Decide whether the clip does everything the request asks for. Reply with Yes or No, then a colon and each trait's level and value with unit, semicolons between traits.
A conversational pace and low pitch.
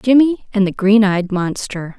No: average, 180 wpm; high, 210 Hz